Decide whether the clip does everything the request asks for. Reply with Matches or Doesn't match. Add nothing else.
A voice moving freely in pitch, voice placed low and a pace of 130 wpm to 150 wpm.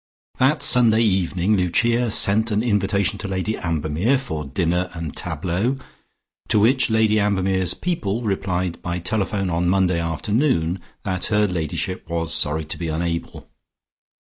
Doesn't match